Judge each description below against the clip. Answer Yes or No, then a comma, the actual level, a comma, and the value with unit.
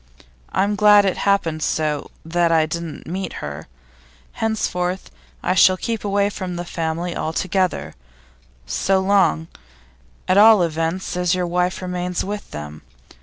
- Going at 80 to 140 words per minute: Yes, slow, 135 wpm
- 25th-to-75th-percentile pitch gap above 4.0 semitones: No, average, 3.1 semitones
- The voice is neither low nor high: Yes, medium, 180 Hz